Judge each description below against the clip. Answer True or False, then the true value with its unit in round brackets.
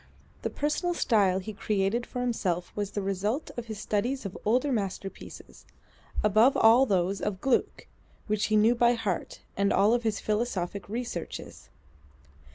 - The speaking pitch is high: True (215 Hz)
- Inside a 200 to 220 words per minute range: False (150 wpm)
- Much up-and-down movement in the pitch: False (3.4 semitones)